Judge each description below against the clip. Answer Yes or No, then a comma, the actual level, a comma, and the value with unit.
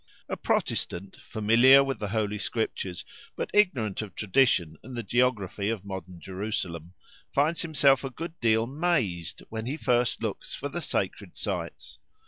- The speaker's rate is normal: Yes, average, 150 wpm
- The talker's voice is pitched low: Yes, low, 110 Hz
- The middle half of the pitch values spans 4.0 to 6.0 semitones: Yes, wide, 5.5 semitones